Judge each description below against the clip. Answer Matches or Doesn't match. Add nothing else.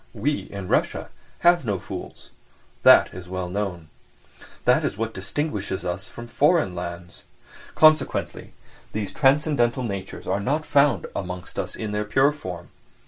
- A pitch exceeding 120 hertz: Doesn't match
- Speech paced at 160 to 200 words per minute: Doesn't match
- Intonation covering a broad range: Matches